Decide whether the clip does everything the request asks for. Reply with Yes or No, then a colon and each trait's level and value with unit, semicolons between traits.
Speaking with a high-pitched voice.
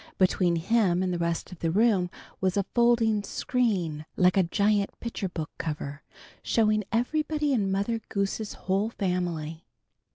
Yes: high, 195 Hz